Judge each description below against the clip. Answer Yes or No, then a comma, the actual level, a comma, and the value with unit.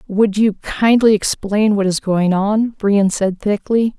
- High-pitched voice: Yes, high, 205 Hz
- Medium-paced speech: Yes, average, 165 wpm